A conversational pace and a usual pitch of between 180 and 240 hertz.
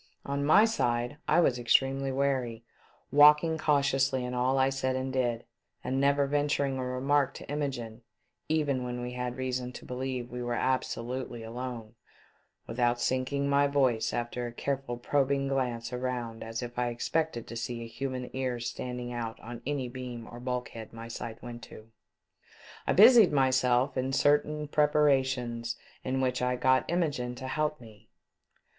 No: average, 165 wpm; low, 130 Hz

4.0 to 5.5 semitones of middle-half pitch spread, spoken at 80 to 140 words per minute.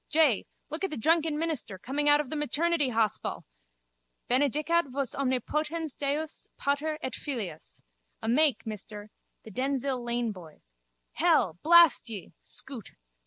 Yes: average, 5.1 semitones; slow, 135 wpm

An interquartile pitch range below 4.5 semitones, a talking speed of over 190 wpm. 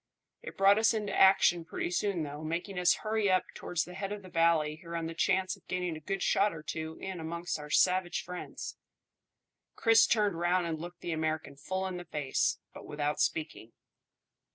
Yes: average, 3.1 semitones; average, 200 wpm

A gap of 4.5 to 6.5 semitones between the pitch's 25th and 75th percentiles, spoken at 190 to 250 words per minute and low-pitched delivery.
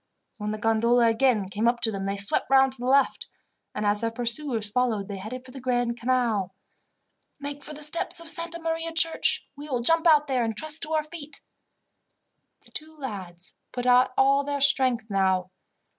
No: average, 4.8 semitones; average, 195 wpm; very high, 250 Hz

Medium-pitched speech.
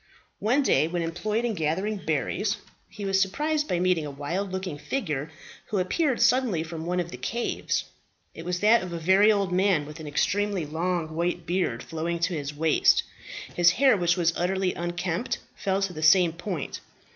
Yes: medium, 180 Hz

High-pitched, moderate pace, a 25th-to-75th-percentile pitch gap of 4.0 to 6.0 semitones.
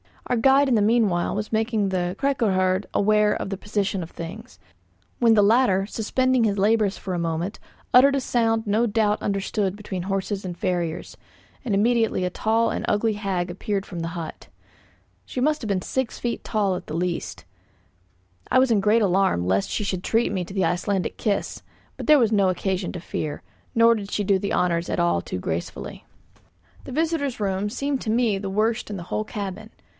No: high, 205 Hz; average, 195 wpm; average, 3.5 semitones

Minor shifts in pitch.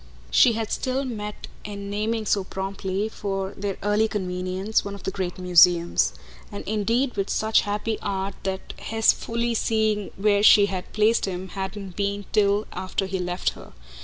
Yes: narrow, 2.2 semitones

